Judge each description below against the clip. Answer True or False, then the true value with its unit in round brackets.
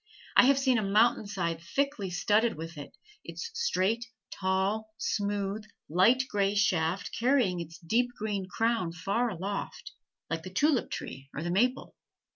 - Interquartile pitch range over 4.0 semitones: True (4.7 semitones)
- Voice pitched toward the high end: True (205 Hz)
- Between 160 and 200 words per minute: False (150 wpm)